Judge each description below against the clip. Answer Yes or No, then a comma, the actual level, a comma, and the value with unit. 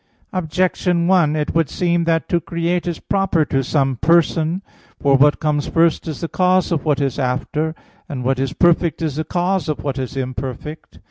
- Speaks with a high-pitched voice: No, medium, 160 Hz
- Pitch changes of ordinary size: Yes, average, 3.5 semitones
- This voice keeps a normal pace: Yes, average, 190 wpm